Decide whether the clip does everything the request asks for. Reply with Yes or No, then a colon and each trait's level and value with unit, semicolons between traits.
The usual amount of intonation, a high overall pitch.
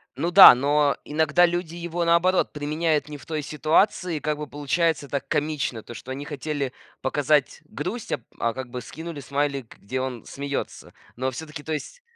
No: average, 3.0 semitones; medium, 150 Hz